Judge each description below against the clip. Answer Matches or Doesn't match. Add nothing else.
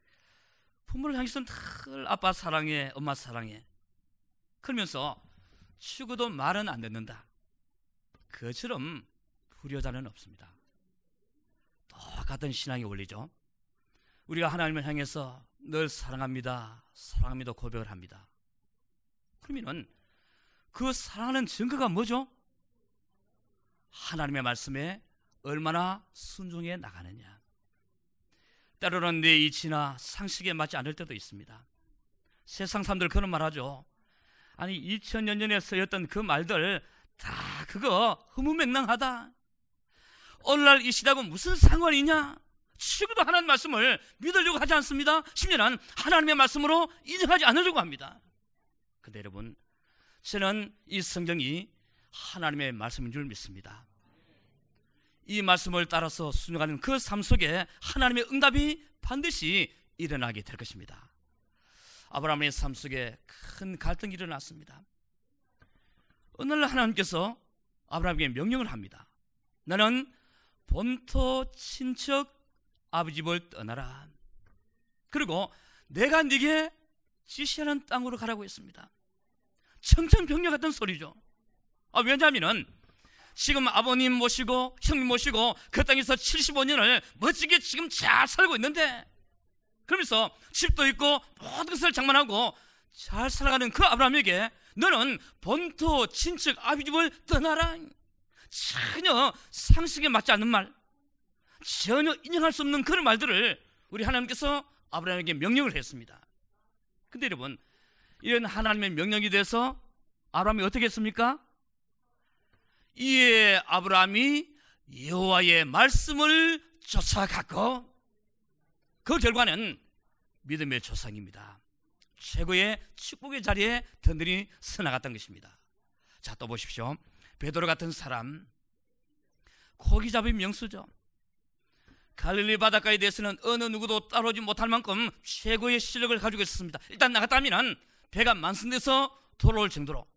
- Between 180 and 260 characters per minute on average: Doesn't match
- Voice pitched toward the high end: Matches